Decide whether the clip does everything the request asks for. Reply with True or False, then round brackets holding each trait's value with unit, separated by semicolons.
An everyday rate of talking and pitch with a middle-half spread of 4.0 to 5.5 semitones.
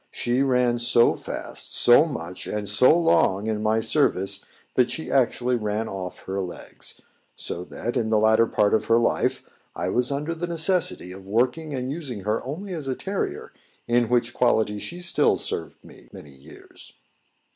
True (175 wpm; 4.7 semitones)